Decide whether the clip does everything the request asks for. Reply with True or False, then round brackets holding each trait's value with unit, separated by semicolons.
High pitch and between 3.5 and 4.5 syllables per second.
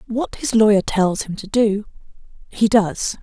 True (210 Hz; 4.2 syllables/s)